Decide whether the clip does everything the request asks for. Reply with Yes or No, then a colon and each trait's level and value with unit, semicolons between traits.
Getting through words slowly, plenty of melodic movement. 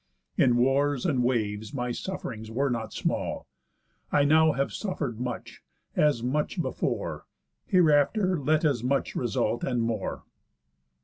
No: slow, 130 wpm; average, 3.9 semitones